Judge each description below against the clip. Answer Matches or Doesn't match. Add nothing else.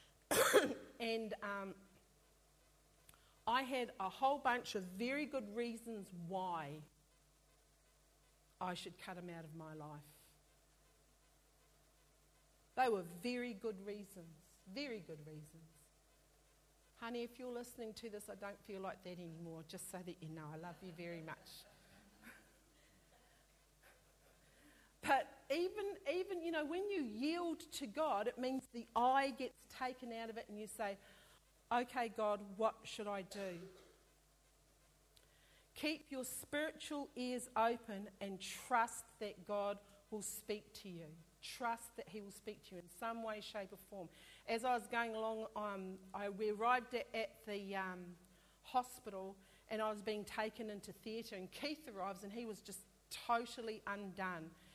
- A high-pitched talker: Matches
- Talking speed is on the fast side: Doesn't match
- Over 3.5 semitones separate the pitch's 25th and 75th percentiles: Matches